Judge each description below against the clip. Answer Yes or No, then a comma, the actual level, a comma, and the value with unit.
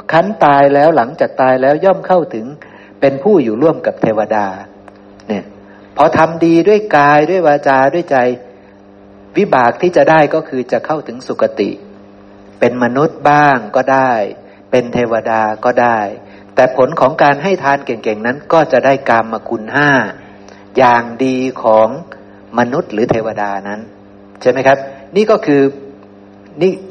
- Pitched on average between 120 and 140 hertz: Yes, low, 125 Hz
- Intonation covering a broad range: Yes, wide, 6.1 semitones